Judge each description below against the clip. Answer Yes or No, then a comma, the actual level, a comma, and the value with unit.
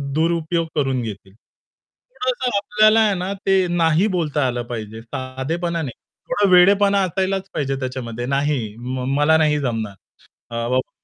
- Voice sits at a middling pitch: Yes, medium, 150 Hz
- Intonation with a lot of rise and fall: Yes, wide, 6.8 semitones